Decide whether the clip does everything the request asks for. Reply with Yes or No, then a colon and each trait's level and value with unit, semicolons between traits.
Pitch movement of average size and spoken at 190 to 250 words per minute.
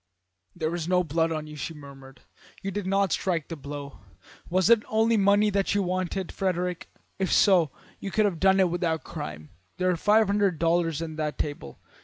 Yes: average, 3.8 semitones; average, 195 wpm